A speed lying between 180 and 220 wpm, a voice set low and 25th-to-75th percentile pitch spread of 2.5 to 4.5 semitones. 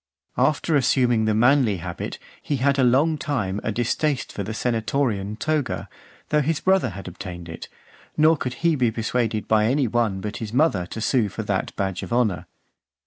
No: average, 185 wpm; low, 120 Hz; average, 5.0 semitones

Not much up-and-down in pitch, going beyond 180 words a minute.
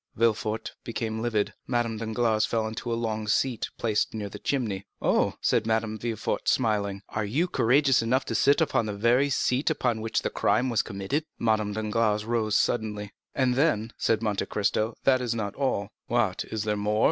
Yes: narrow, 2.1 semitones; average, 195 wpm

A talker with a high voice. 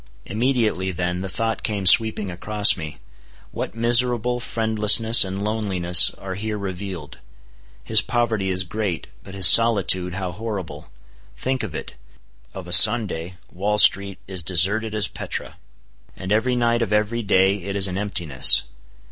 No: low, 100 Hz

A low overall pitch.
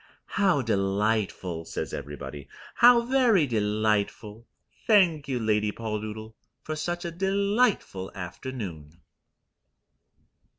Yes: low, 110 Hz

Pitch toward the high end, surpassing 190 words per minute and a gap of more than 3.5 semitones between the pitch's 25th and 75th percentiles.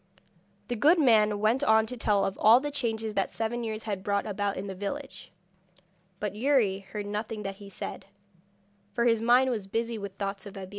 No: high, 215 Hz; average, 200 wpm; average, 2.8 semitones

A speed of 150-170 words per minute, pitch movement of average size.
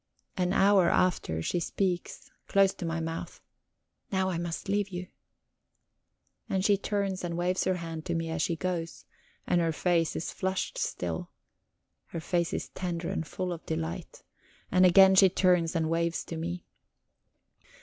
No: average, 160 wpm; narrow, 2.3 semitones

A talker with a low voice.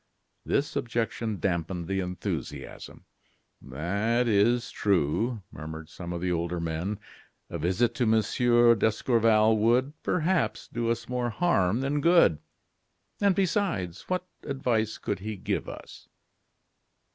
Yes: low, 110 Hz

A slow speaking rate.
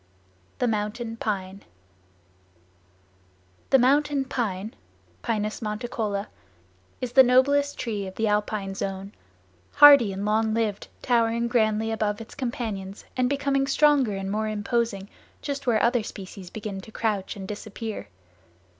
Yes: slow, 125 wpm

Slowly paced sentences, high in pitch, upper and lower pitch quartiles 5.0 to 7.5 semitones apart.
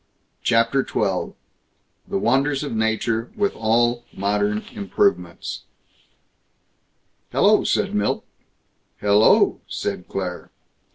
No: slow, 95 wpm; low, 115 Hz; average, 5.3 semitones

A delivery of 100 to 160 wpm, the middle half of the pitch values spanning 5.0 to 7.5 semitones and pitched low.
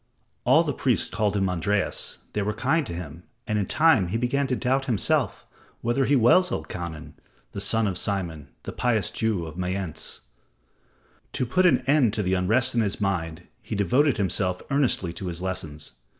No: average, 180 wpm; wide, 5.4 semitones; low, 100 Hz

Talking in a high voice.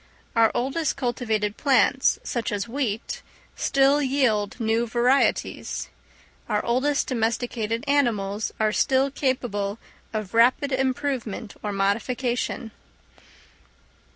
Yes: high, 240 Hz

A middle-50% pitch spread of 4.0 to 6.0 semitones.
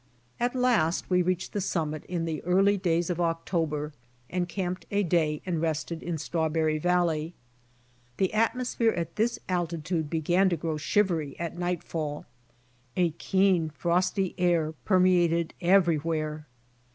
No: narrow, 2.5 semitones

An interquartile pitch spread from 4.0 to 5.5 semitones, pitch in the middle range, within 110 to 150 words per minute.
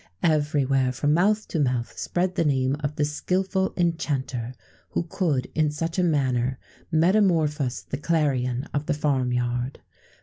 Yes: average, 4.3 semitones; medium, 150 Hz; average, 145 wpm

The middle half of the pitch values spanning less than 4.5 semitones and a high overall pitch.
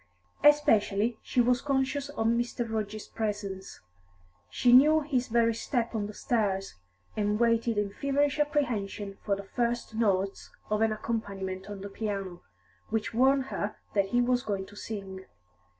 Yes: average, 3.4 semitones; high, 220 Hz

